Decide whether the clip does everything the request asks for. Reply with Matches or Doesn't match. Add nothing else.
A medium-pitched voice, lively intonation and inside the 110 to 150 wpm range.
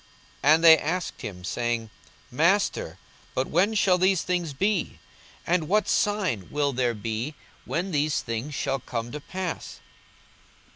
Matches